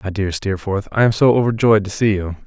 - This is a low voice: Yes, low, 105 Hz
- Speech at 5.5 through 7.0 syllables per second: Yes, 5.8 syllables/s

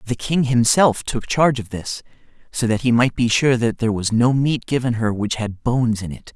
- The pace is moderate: No, fast, 235 wpm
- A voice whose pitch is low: Yes, low, 120 Hz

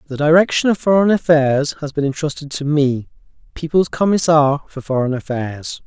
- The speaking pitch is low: No, medium, 150 Hz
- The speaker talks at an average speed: Yes, average, 155 wpm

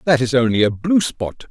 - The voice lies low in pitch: Yes, low, 130 Hz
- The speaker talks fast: Yes, fast, 240 wpm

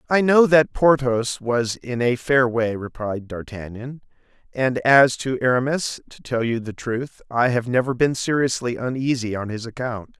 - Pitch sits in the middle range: No, low, 125 Hz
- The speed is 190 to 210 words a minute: No, average, 170 wpm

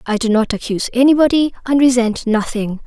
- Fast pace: No, average, 170 wpm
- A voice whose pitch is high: Yes, high, 240 Hz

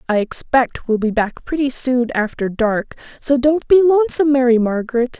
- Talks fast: No, average, 175 wpm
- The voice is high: Yes, very high, 255 Hz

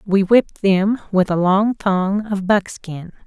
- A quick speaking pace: No, average, 165 wpm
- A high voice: Yes, high, 195 Hz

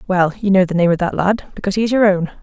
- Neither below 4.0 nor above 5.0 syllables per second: No, 7.1 syllables/s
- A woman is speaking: Yes, female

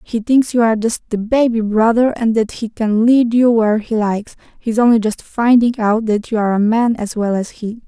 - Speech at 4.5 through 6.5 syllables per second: Yes, 5.2 syllables/s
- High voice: Yes, high, 225 Hz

